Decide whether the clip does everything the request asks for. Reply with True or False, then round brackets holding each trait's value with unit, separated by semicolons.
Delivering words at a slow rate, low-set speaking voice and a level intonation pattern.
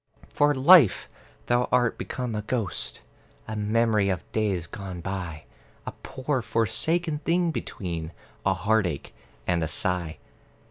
False (130 wpm; 105 Hz; 5.5 semitones)